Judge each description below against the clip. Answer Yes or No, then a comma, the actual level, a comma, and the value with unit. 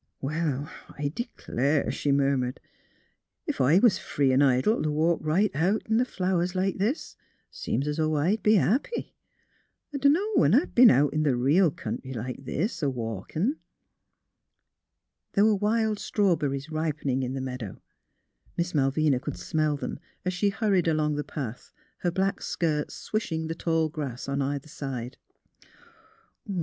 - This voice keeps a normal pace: Yes, average, 160 wpm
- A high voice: No, medium, 155 Hz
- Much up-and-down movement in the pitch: Yes, wide, 5.8 semitones